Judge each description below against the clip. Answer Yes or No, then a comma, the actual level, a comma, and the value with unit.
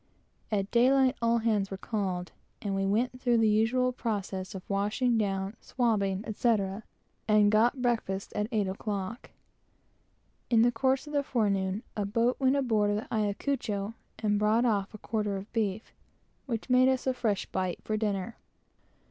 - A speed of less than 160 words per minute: No, average, 165 wpm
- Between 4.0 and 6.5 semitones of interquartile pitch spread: No, average, 3.3 semitones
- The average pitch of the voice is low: No, high, 215 Hz